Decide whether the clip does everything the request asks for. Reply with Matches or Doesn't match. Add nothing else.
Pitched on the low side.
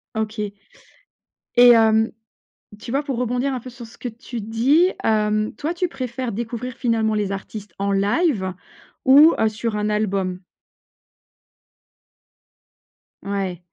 Doesn't match